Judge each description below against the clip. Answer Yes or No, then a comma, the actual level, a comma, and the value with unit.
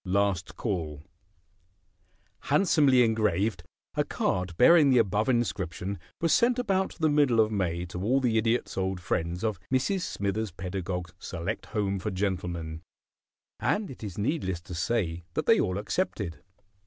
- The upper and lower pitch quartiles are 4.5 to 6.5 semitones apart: Yes, wide, 5.5 semitones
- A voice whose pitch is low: Yes, low, 100 Hz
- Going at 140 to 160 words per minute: Yes, average, 150 wpm